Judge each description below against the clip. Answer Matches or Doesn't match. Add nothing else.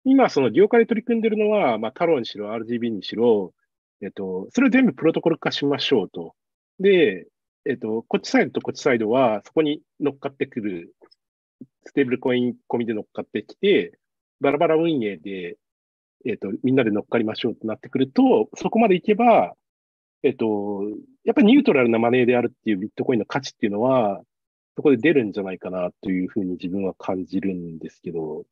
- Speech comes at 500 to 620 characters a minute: Doesn't match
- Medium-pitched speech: Doesn't match